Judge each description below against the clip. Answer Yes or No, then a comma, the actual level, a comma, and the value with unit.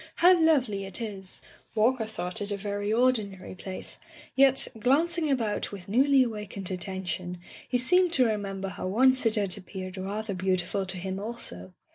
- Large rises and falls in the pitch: No, average, 5.0 semitones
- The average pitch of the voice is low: No, high, 205 Hz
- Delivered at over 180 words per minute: No, average, 165 wpm